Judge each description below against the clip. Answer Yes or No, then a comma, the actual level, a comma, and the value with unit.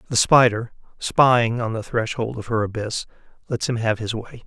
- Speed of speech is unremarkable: Yes, average, 190 wpm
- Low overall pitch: Yes, low, 115 Hz